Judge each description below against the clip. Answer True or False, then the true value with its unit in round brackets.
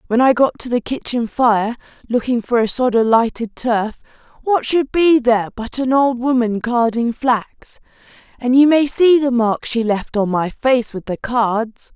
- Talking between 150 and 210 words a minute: True (190 wpm)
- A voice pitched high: True (240 Hz)